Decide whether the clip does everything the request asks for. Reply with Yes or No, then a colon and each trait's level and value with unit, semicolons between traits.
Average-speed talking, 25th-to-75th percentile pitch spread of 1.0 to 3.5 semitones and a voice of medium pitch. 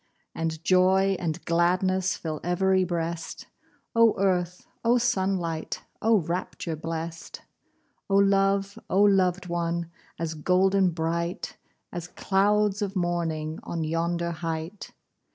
No: slow, 115 wpm; narrow, 2.6 semitones; medium, 180 Hz